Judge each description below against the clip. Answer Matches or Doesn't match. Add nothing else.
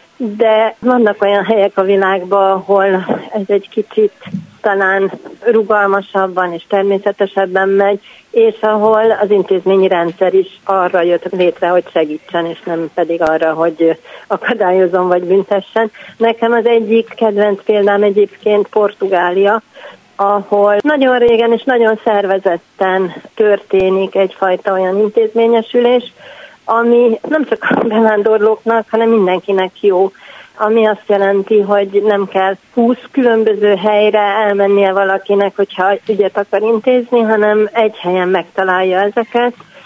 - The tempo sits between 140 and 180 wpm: Doesn't match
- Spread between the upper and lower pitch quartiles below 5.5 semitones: Matches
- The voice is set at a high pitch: Matches